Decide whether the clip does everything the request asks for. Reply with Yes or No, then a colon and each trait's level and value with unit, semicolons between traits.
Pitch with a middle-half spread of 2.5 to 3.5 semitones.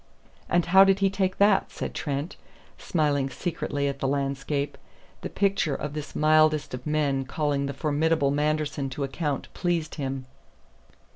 Yes: average, 2.8 semitones